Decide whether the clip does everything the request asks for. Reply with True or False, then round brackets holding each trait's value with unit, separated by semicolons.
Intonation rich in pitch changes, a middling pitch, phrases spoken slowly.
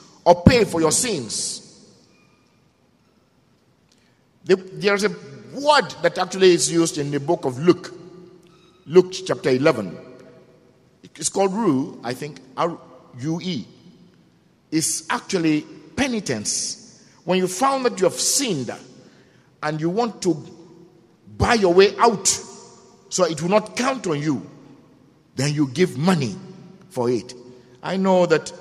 False (3.7 semitones; 175 Hz; 125 wpm)